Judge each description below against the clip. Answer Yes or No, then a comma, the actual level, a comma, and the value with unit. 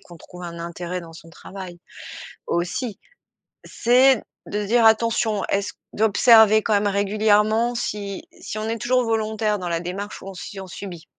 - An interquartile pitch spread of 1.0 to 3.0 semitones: No, average, 3.4 semitones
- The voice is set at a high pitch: Yes, high, 205 Hz